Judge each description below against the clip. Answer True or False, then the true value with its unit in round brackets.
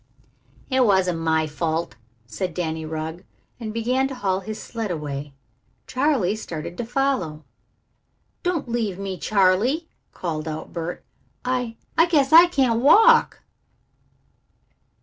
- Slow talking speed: True (125 wpm)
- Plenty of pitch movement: True (7.8 semitones)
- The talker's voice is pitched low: False (200 Hz)